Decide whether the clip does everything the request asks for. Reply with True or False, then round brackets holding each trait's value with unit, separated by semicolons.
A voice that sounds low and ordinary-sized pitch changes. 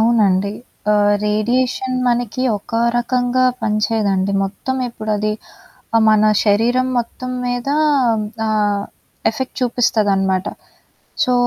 False (220 Hz; 3.1 semitones)